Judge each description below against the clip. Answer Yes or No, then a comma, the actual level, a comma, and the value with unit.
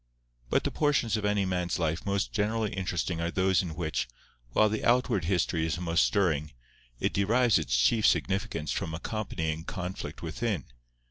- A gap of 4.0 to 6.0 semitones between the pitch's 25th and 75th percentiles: Yes, average, 4.3 semitones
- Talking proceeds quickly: No, average, 160 wpm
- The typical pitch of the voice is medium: No, very low, 95 Hz